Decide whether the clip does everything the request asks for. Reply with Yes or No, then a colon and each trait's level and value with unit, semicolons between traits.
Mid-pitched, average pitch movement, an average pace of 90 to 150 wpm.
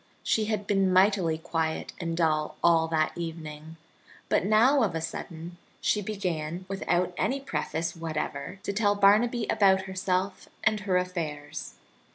Yes: medium, 180 Hz; average, 3.7 semitones; average, 145 wpm